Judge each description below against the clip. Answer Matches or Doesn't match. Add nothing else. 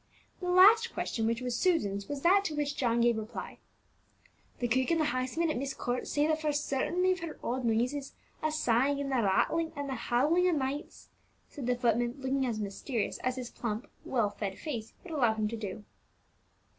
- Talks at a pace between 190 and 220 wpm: Matches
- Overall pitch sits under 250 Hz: Doesn't match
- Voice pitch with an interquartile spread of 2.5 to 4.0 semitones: Doesn't match